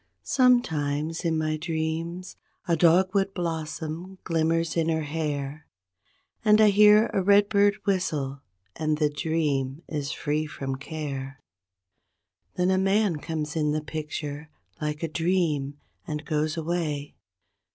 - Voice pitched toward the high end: No, medium, 160 Hz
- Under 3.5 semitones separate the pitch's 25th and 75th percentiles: Yes, average, 3.1 semitones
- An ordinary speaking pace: No, slow, 130 wpm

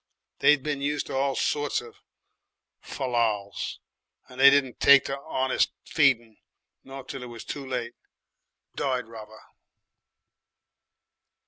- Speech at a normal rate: No, slow, 120 wpm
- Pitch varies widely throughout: No, average, 2.9 semitones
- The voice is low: Yes, low, 130 Hz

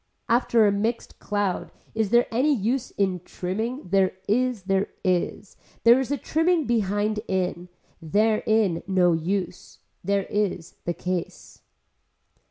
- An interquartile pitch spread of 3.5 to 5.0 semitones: Yes, average, 3.9 semitones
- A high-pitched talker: Yes, high, 205 Hz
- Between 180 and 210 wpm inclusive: No, average, 140 wpm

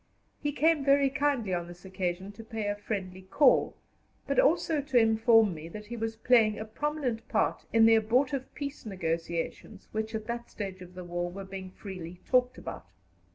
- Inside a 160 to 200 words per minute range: Yes, average, 185 wpm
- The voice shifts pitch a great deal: No, average, 5.0 semitones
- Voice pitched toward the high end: Yes, high, 220 Hz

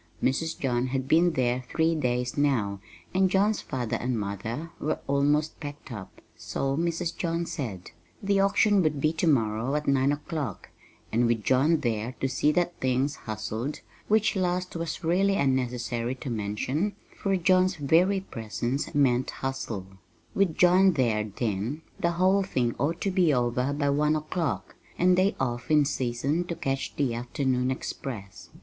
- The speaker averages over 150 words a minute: Yes, average, 160 wpm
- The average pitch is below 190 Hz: Yes, medium, 140 Hz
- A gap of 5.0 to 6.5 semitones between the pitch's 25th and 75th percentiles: Yes, wide, 5.6 semitones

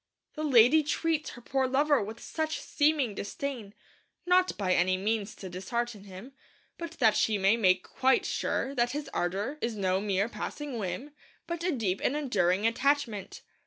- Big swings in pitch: Yes, wide, 6.5 semitones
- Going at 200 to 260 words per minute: No, average, 165 wpm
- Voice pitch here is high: Yes, high, 235 Hz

